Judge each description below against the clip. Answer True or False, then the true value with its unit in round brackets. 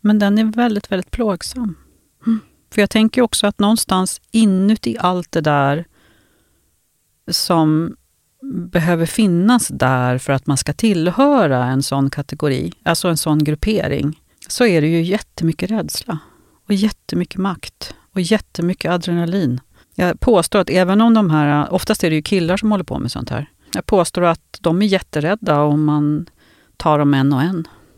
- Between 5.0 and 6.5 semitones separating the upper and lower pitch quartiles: True (5.5 semitones)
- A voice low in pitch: False (175 Hz)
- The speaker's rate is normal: True (165 wpm)